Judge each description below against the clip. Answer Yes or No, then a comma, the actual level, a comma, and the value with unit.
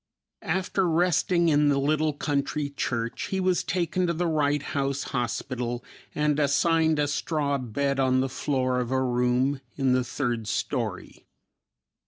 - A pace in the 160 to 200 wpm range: No, average, 150 wpm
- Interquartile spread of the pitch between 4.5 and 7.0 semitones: No, average, 3.5 semitones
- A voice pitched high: No, medium, 140 Hz